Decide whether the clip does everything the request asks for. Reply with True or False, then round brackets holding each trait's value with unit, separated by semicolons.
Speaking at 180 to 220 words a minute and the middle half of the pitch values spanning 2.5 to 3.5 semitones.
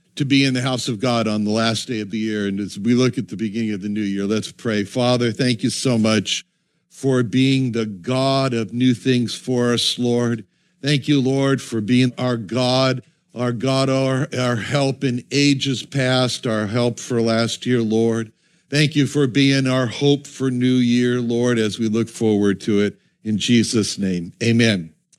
True (200 wpm; 2.9 semitones)